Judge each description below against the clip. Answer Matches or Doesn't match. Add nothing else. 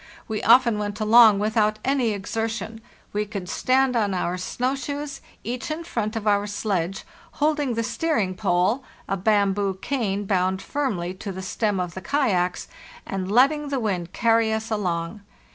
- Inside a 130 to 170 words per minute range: Matches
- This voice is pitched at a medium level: Doesn't match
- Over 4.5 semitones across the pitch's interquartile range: Doesn't match